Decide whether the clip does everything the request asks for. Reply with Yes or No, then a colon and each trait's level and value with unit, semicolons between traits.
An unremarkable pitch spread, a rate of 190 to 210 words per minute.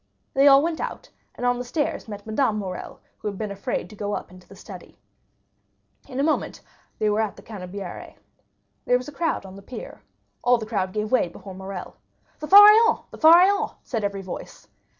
No: wide, 5.9 semitones; average, 200 wpm